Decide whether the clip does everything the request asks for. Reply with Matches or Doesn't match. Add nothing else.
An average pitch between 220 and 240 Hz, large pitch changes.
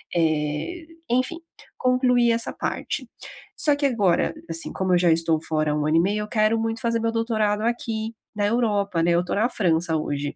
Doesn't match